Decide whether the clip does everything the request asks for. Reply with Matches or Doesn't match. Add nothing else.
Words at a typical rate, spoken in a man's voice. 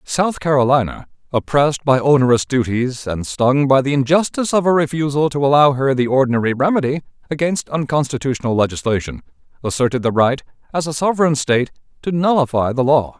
Matches